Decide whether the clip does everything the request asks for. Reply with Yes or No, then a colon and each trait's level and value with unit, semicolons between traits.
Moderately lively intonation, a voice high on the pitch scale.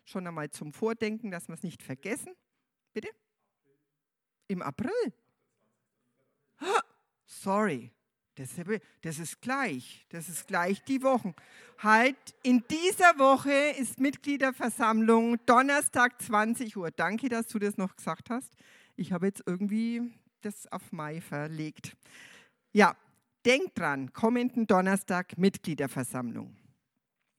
No: wide, 6.6 semitones; high, 215 Hz